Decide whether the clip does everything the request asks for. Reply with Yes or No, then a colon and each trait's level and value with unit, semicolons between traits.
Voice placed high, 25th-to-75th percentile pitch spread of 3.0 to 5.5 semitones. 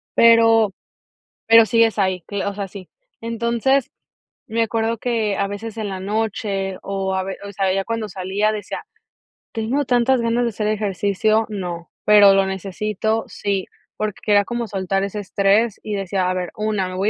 No: high, 210 Hz; narrow, 2.6 semitones